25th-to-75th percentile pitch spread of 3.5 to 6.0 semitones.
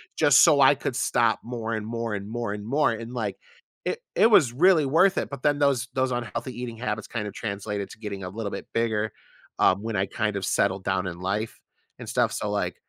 Yes: average, 3.9 semitones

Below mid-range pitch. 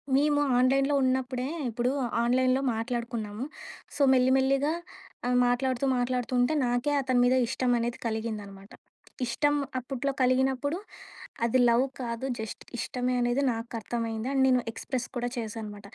No: very high, 250 Hz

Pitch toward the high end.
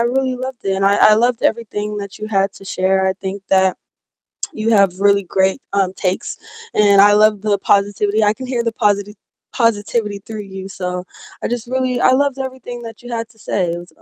Yes: high, 205 Hz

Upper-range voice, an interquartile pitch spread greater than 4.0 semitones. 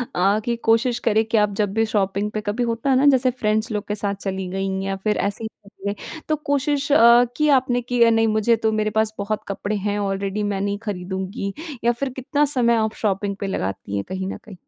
No: high, 210 Hz; average, 2.7 semitones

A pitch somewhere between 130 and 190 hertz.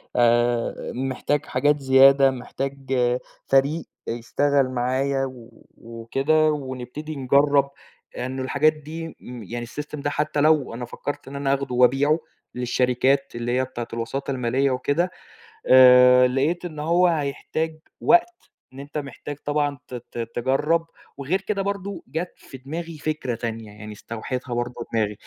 Yes: low, 135 Hz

